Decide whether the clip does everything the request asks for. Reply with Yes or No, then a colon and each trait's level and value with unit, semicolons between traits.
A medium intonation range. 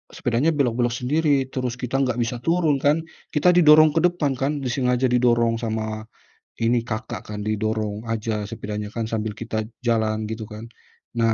Yes: average, 3.6 semitones